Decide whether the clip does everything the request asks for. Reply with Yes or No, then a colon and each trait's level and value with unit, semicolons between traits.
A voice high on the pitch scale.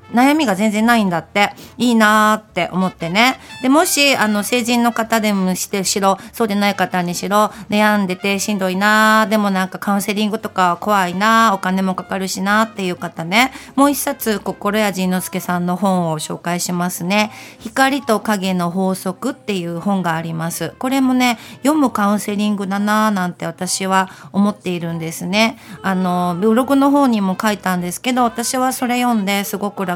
Yes: high, 205 Hz